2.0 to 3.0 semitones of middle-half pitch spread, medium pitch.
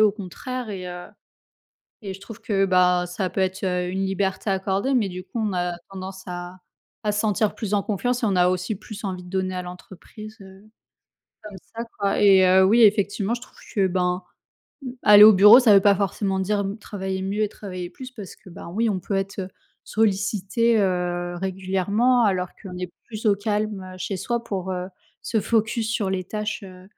No: narrow, 2.4 semitones; high, 195 Hz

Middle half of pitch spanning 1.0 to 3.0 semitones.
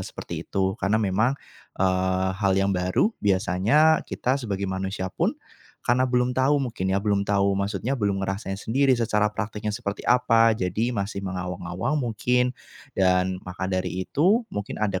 No: average, 4.1 semitones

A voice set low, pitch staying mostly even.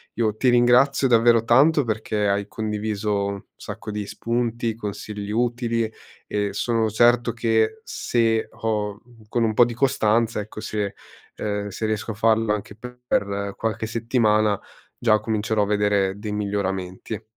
Yes: low, 110 Hz; narrow, 2.1 semitones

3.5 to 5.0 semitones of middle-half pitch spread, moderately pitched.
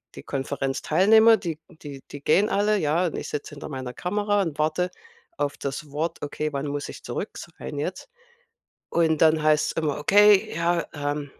Yes: average, 4.0 semitones; medium, 155 Hz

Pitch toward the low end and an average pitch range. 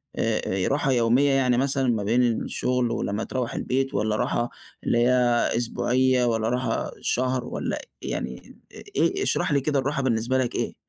No: low, 125 Hz; narrow, 2.1 semitones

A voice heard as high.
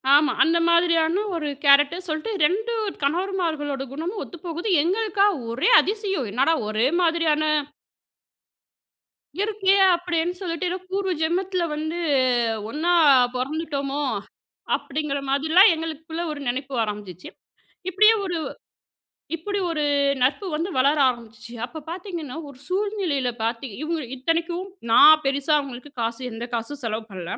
Yes: very high, 315 Hz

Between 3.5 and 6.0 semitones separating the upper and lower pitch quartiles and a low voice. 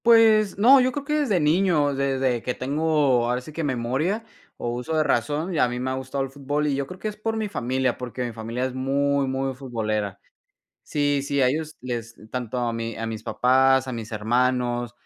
Yes: average, 3.9 semitones; low, 130 Hz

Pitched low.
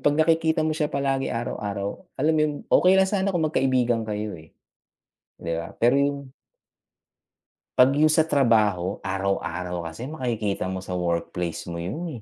Yes: low, 120 Hz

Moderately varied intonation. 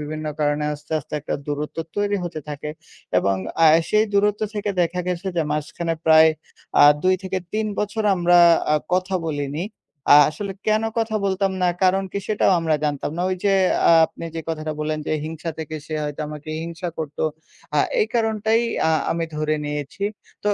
Yes: average, 4.5 semitones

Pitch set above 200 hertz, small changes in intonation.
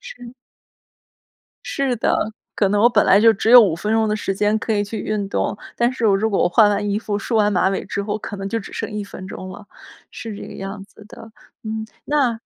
Yes: high, 210 Hz; narrow, 1.9 semitones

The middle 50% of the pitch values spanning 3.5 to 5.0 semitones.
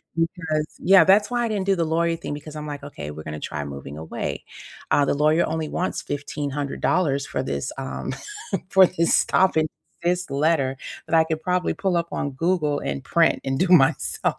Yes: average, 3.8 semitones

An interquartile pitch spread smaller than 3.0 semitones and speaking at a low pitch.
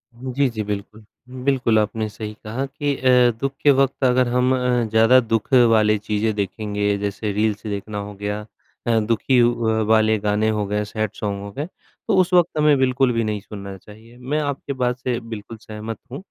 No: average, 3.3 semitones; low, 110 Hz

